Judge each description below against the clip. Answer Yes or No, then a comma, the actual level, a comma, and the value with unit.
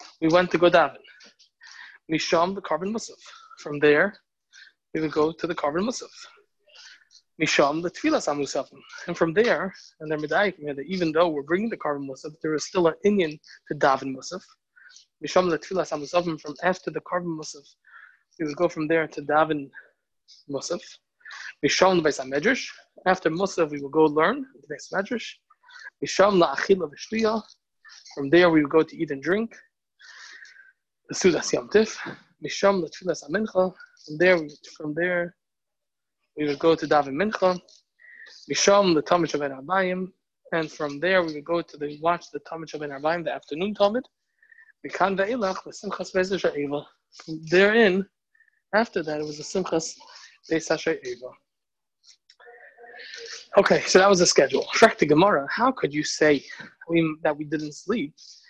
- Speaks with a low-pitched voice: No, medium, 175 Hz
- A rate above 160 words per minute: No, average, 155 wpm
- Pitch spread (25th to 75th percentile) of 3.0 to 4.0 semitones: No, average, 4.5 semitones